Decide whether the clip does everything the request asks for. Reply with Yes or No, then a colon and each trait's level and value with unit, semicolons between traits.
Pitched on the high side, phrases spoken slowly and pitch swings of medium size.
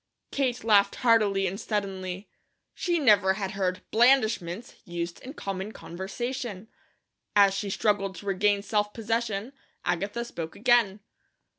Yes: high, 205 Hz; slow, 125 wpm; average, 3.2 semitones